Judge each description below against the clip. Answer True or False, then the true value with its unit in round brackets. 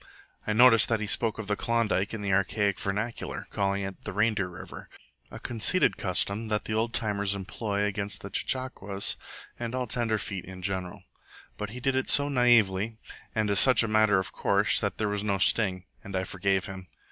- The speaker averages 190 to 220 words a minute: True (195 wpm)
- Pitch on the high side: False (105 Hz)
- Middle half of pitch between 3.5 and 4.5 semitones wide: False (2.7 semitones)